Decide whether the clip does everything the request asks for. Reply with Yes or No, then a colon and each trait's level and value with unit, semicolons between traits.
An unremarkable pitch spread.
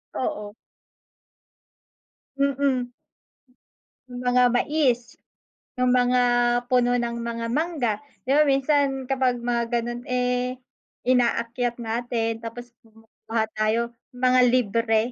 No: narrow, 1.5 semitones